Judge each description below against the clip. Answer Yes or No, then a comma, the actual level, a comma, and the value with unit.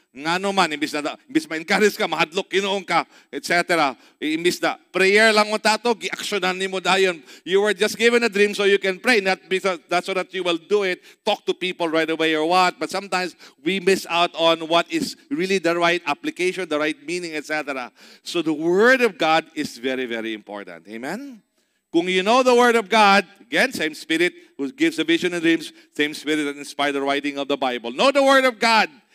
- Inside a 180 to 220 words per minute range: Yes, average, 185 wpm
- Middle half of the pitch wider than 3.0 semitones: Yes, average, 5.1 semitones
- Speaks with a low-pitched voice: No, medium, 185 Hz